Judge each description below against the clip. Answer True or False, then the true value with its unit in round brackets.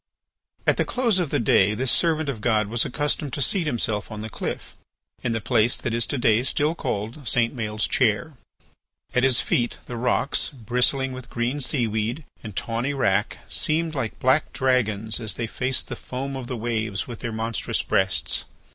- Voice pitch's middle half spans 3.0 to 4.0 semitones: True (3.4 semitones)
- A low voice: True (120 Hz)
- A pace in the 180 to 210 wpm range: True (185 wpm)